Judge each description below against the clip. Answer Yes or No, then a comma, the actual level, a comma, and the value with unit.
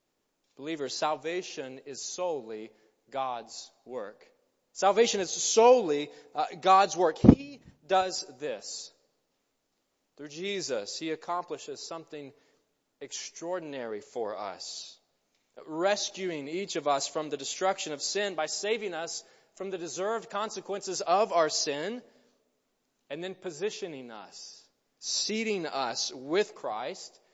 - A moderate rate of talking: No, slow, 110 wpm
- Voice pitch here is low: No, medium, 185 Hz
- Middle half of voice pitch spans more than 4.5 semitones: Yes, average, 5.0 semitones